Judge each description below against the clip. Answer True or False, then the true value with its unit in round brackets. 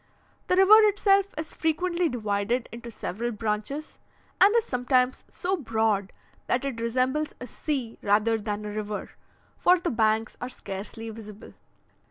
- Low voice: False (240 Hz)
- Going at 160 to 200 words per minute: False (145 wpm)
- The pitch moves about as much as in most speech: False (6.2 semitones)